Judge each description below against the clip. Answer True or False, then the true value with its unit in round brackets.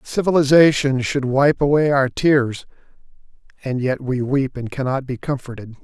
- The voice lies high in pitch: False (135 Hz)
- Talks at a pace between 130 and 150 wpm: True (145 wpm)